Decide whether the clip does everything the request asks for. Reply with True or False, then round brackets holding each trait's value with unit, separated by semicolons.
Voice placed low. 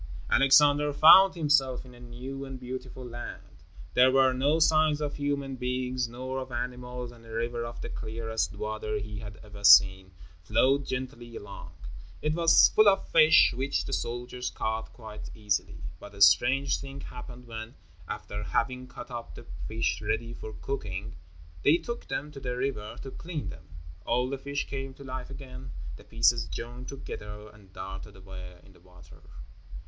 True (125 Hz)